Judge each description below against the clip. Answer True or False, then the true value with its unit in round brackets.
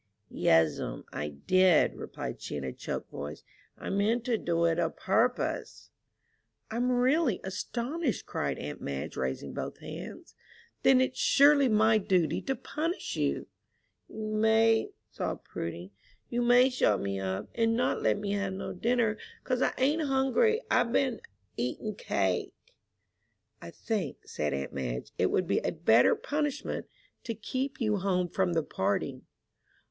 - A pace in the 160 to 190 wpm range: False (150 wpm)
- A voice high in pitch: True (215 Hz)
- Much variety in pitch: True (8.1 semitones)